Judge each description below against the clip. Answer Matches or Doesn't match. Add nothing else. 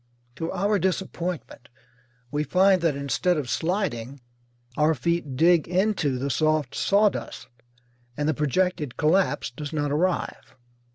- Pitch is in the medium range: Matches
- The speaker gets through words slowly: Matches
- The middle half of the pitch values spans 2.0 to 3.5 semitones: Doesn't match